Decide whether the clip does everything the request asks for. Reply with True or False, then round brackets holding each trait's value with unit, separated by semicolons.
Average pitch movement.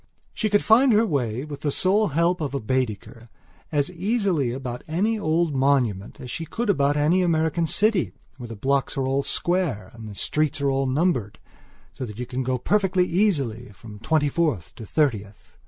False (6.2 semitones)